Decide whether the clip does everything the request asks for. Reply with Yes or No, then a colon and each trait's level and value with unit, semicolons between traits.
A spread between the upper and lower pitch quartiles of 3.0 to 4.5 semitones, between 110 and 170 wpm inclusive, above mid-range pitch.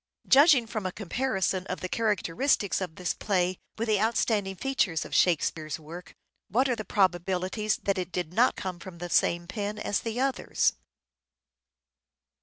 Yes: average, 3.9 semitones; average, 160 wpm; high, 195 Hz